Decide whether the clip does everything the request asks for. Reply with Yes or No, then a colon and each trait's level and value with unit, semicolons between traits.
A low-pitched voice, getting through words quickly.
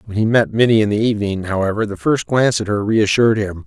Yes: low, 110 Hz; fast, 245 wpm